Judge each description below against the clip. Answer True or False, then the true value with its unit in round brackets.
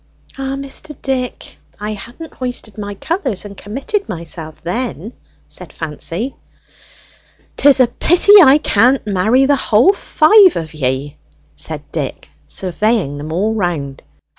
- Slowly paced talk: True (130 wpm)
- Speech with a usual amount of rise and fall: False (7.9 semitones)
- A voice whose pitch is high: True (220 Hz)